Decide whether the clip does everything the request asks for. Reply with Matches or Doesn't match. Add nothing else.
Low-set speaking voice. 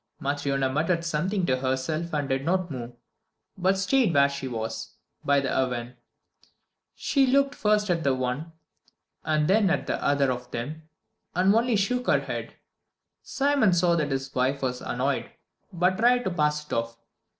Doesn't match